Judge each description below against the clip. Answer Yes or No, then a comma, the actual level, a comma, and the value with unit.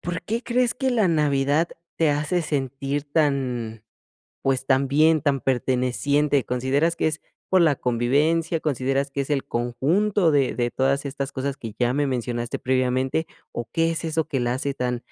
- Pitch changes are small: No, average, 3.6 semitones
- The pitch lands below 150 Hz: Yes, medium, 140 Hz